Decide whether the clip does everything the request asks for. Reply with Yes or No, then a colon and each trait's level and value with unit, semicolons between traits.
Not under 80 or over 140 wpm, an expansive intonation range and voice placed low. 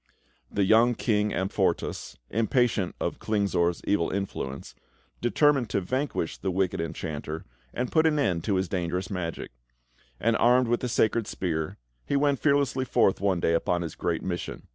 No: average, 160 wpm; wide, 5.8 semitones; low, 100 Hz